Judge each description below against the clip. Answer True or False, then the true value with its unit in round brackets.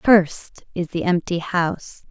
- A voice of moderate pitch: True (175 Hz)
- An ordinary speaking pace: True (145 wpm)